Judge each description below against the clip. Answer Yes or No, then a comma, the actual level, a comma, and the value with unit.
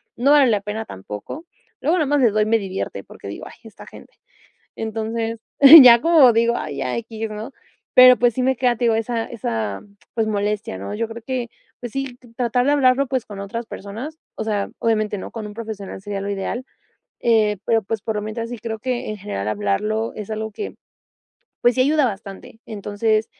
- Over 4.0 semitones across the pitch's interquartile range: No, average, 2.8 semitones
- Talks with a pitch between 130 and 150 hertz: No, high, 225 Hz